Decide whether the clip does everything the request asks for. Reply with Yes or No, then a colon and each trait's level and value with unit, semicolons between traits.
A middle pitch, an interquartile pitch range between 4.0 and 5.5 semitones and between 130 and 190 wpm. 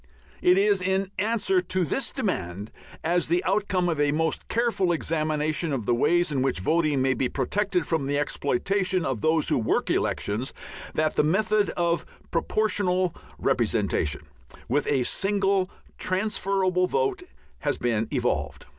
Yes: medium, 175 Hz; average, 5.1 semitones; average, 145 wpm